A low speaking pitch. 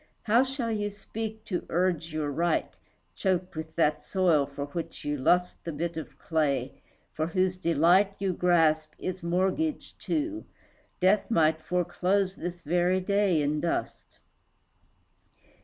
No: medium, 175 Hz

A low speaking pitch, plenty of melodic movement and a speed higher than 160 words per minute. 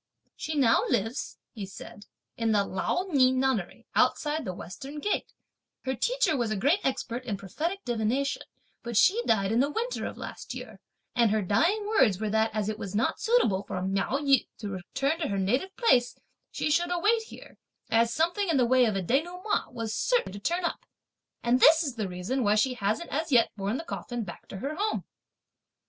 No: very high, 250 Hz; wide, 7.1 semitones; average, 200 wpm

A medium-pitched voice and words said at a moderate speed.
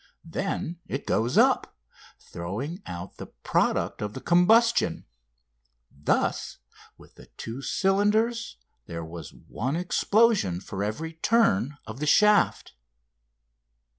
No: medium, 160 Hz; slow, 105 wpm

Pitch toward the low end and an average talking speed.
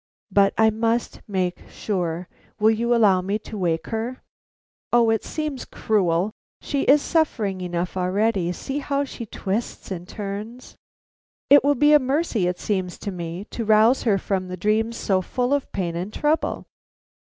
No: high, 215 Hz; average, 165 wpm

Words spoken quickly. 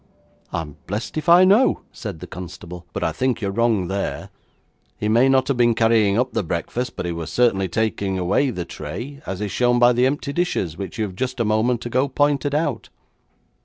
Yes: fast, 210 wpm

